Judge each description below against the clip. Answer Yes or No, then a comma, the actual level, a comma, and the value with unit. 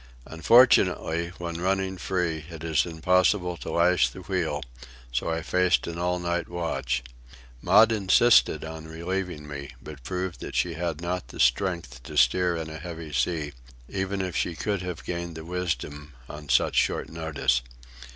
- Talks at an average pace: Yes, average, 160 wpm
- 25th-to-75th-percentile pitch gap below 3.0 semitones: Yes, narrow, 2.4 semitones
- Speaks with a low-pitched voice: Yes, very low, 85 Hz